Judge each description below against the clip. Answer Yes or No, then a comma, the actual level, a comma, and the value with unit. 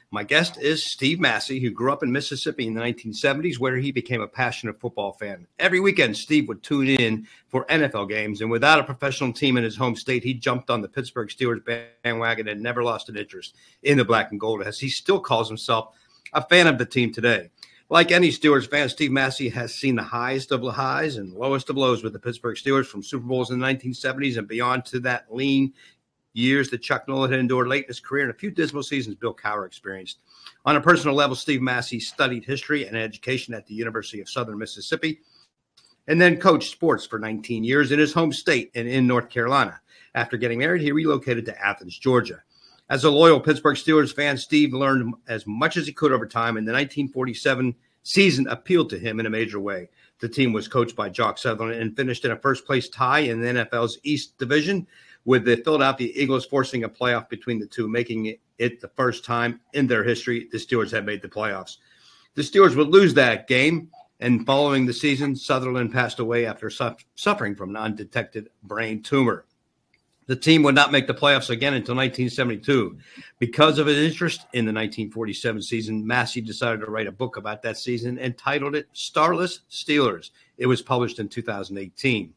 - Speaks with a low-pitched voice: Yes, low, 125 Hz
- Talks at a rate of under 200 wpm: No, fast, 205 wpm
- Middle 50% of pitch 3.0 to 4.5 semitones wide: Yes, average, 3.7 semitones